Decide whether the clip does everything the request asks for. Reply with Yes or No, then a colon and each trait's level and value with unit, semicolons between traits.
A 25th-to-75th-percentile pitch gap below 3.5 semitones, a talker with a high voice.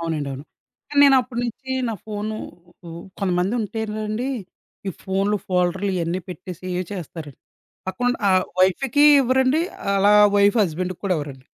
No: average, 3.9 semitones; high, 195 Hz